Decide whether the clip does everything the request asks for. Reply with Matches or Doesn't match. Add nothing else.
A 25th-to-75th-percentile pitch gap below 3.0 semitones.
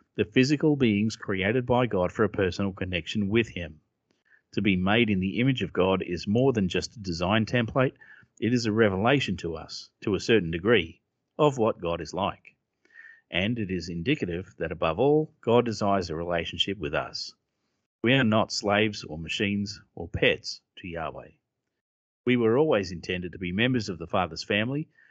Doesn't match